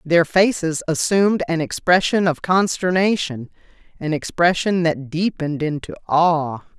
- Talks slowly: Yes, slow, 115 wpm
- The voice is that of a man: No, female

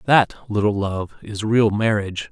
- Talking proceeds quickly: No, average, 155 wpm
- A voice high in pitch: No, low, 105 Hz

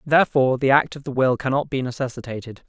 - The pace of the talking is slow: No, average, 200 wpm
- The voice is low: Yes, low, 130 Hz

